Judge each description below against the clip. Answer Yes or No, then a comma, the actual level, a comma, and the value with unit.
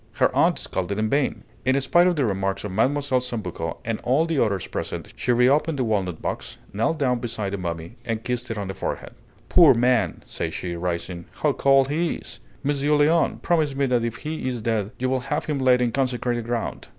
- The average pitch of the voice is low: Yes, low, 125 Hz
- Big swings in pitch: No, average, 4.8 semitones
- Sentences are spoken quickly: Yes, fast, 210 wpm